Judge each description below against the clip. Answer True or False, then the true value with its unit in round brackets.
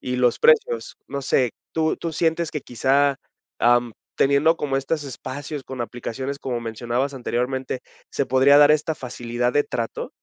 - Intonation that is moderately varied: True (3.2 semitones)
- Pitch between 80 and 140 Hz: True (135 Hz)